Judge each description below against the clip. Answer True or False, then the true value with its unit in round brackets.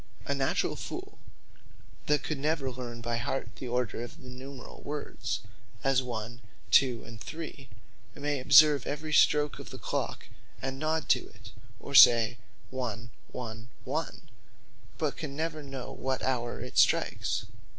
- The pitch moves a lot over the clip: False (3.6 semitones)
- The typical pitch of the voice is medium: False (130 Hz)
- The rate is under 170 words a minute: True (145 wpm)